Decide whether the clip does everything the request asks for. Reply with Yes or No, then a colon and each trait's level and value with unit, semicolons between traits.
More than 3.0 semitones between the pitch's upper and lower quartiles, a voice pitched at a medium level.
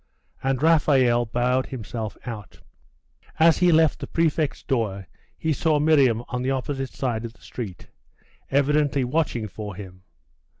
No: average, 4.6 semitones; low, 130 Hz